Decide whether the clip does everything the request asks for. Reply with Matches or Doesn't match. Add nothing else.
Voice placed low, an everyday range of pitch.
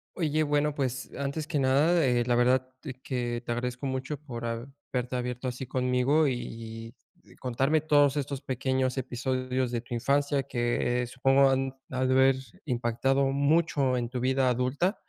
Doesn't match